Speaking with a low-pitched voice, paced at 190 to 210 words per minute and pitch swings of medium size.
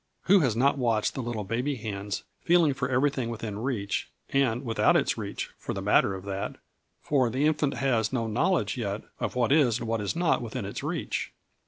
Yes: low, 120 Hz; average, 200 wpm; average, 4.2 semitones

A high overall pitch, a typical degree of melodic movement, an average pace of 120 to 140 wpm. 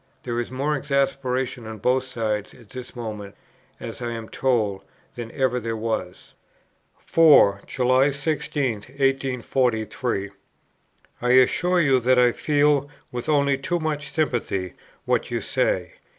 No: low, 125 Hz; average, 3.3 semitones; slow, 135 wpm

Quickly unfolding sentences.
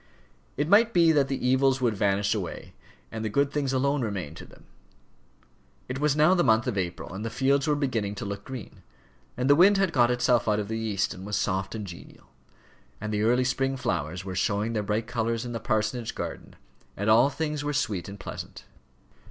Yes: fast, 210 wpm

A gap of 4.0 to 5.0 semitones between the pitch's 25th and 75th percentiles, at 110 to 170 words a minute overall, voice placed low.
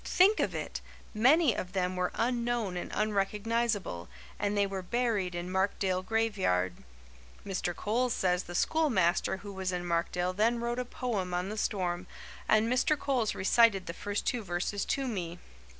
No: average, 4.3 semitones; average, 165 wpm; high, 200 Hz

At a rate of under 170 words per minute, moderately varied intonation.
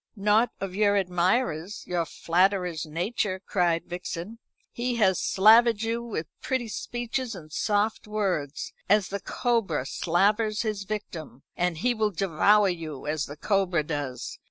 Yes: average, 140 wpm; average, 4.2 semitones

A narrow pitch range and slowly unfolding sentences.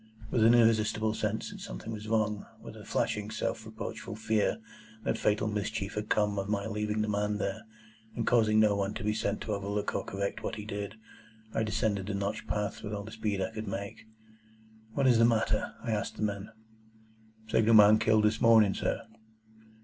No: narrow, 1.3 semitones; average, 190 wpm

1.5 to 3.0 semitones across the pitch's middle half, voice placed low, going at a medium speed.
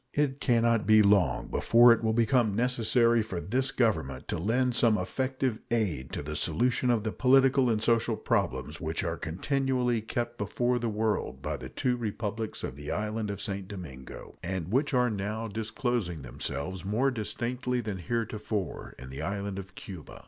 No: average, 4.5 semitones; low, 110 Hz; average, 175 wpm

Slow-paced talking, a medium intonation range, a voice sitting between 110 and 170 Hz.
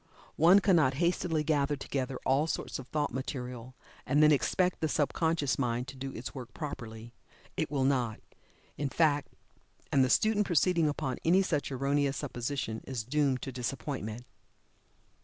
No: average, 155 wpm; average, 3.2 semitones; medium, 140 Hz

